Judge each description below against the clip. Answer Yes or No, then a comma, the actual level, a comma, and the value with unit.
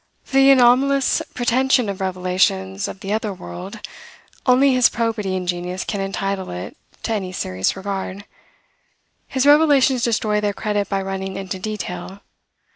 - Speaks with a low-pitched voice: No, high, 200 Hz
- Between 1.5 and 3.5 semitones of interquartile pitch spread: No, average, 4.3 semitones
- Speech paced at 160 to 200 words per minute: No, average, 145 wpm